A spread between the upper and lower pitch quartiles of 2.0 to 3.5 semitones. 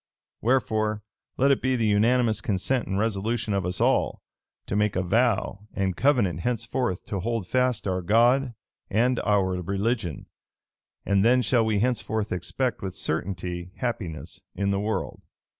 No: average, 3.9 semitones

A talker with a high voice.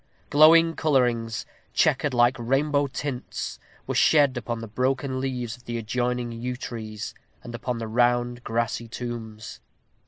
No: low, 120 Hz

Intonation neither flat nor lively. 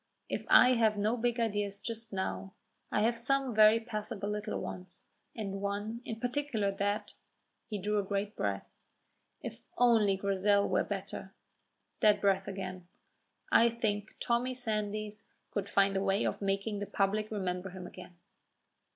No: narrow, 2.2 semitones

